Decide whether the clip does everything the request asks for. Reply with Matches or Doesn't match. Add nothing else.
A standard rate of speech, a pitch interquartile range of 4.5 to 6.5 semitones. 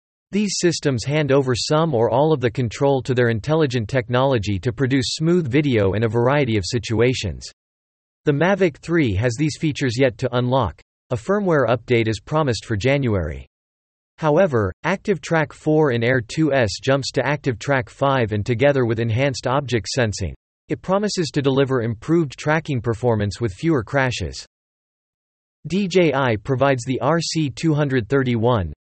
Matches